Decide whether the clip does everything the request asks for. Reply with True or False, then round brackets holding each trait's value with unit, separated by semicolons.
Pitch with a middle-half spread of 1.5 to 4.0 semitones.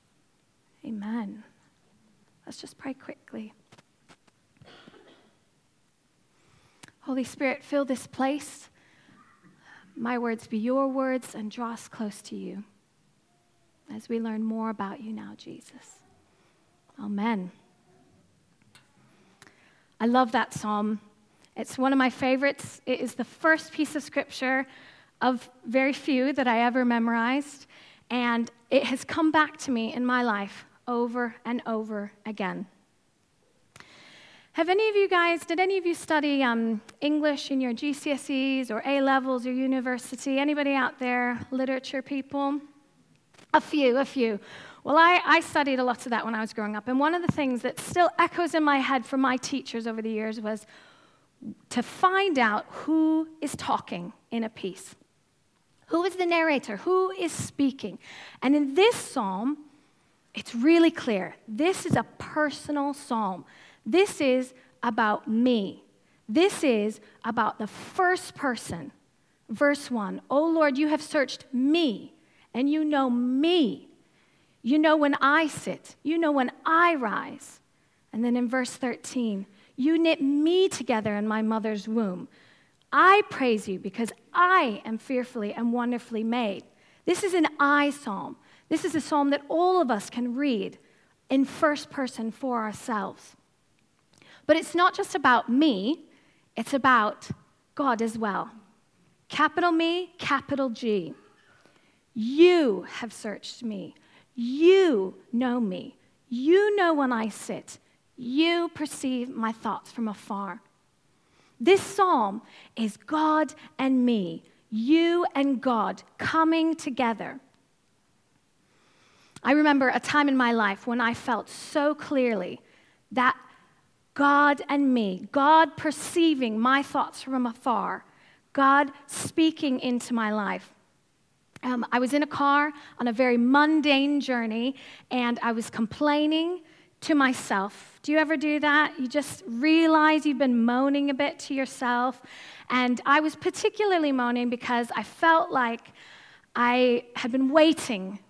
False (4.4 semitones)